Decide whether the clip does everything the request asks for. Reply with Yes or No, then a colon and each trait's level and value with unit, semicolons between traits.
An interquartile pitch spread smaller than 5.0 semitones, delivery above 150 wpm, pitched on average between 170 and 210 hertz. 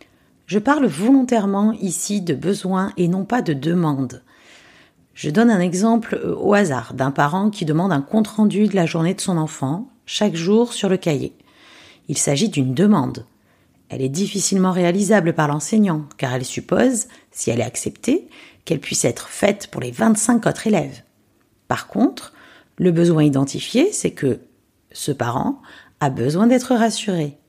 No: wide, 5.6 semitones; average, 160 wpm; high, 190 Hz